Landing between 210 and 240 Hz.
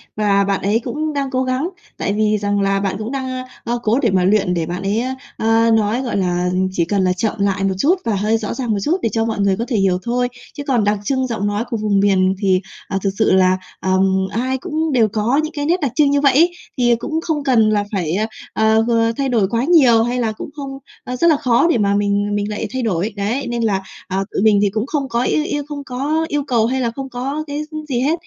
Yes: high, 225 Hz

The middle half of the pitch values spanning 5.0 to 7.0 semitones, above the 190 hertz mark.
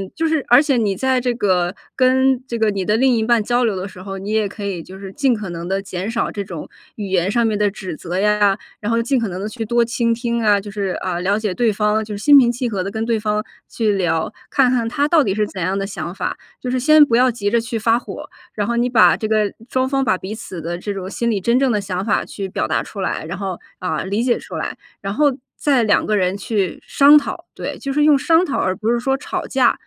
No: average, 3.8 semitones; high, 215 Hz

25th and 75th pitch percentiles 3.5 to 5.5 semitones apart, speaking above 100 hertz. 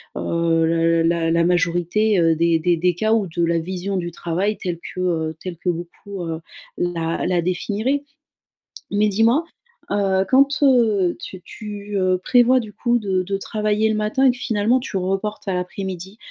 Yes: average, 3.8 semitones; high, 190 Hz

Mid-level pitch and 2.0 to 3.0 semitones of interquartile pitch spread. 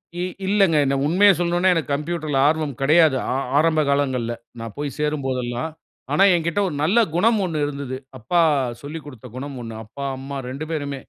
No: medium, 150 Hz; average, 3.6 semitones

